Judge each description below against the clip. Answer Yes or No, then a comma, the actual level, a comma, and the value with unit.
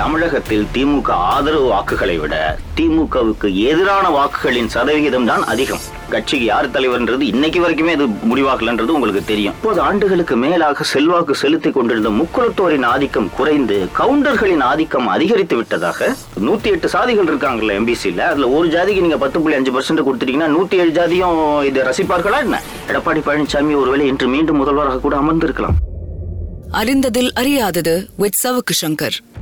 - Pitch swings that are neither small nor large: No, wide, 6.4 semitones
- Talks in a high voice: No, medium, 155 Hz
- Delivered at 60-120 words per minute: No, fast, 130 wpm